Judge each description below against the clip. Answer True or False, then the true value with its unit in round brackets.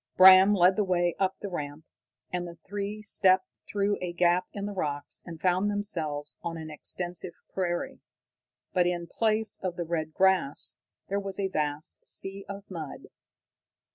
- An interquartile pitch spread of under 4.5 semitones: True (2.7 semitones)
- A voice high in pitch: False (180 Hz)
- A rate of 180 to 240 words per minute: False (165 wpm)